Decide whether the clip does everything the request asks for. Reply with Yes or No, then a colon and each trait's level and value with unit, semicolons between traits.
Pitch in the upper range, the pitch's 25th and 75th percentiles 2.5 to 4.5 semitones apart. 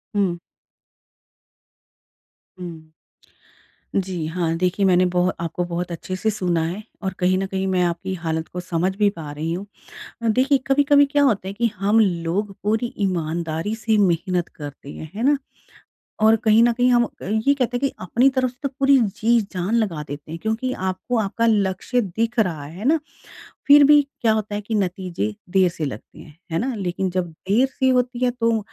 No: high, 195 Hz; average, 4.9 semitones